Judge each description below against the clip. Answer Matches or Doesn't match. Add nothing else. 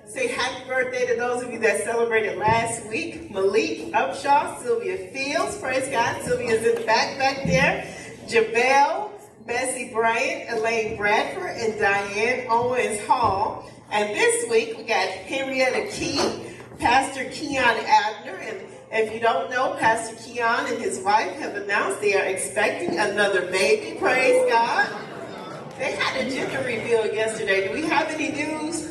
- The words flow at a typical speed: Matches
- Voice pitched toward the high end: Matches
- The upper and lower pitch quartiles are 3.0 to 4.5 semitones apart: Doesn't match